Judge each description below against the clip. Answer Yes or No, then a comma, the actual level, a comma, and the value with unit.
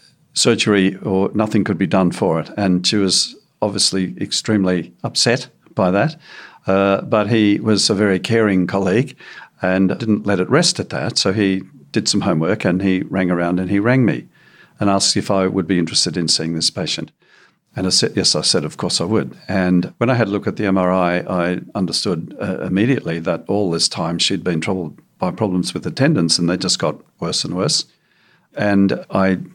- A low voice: Yes, very low, 95 Hz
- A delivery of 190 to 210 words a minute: Yes, average, 200 wpm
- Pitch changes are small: Yes, narrow, 2.1 semitones